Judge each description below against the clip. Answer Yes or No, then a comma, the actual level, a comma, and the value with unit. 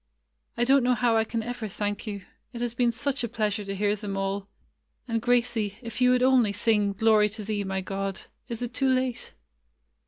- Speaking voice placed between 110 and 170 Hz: No, high, 225 Hz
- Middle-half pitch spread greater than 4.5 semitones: No, average, 3.0 semitones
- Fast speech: Yes, fast, 210 wpm